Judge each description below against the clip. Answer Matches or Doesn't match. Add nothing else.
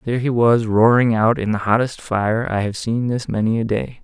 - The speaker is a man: Matches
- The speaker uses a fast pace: Matches